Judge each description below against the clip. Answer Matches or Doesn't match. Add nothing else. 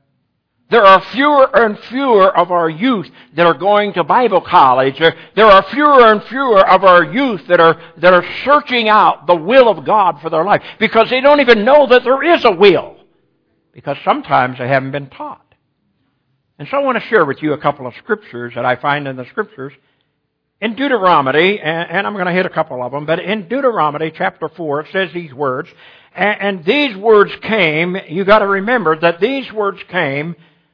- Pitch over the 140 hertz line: Matches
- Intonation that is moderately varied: Doesn't match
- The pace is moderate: Matches